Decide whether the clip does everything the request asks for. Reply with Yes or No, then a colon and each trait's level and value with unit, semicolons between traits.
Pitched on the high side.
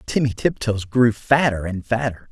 No: low, 115 Hz